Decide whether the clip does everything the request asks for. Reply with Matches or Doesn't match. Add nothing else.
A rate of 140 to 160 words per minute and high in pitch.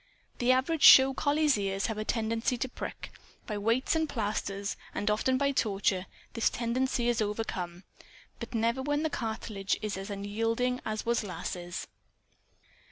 Matches